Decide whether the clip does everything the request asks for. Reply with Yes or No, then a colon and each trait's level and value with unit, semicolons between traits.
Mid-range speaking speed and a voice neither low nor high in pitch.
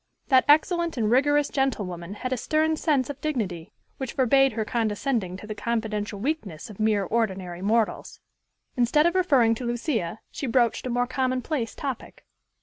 No: average, 160 wpm; high, 240 Hz